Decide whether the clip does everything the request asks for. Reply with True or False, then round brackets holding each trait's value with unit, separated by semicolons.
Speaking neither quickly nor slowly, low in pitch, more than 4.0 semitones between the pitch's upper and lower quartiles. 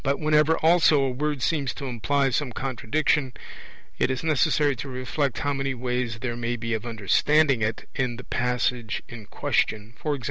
False (175 wpm; 130 Hz; 3.5 semitones)